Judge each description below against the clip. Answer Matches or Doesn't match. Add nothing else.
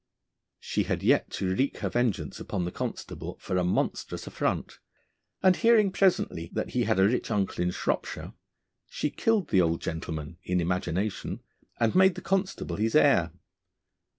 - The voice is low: Matches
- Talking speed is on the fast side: Doesn't match